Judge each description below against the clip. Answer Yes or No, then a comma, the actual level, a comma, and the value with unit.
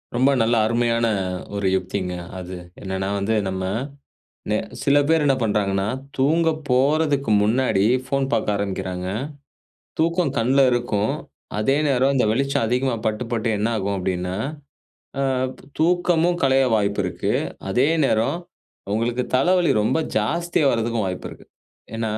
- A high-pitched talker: No, low, 115 Hz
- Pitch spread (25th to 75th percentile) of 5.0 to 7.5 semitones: Yes, average, 5.3 semitones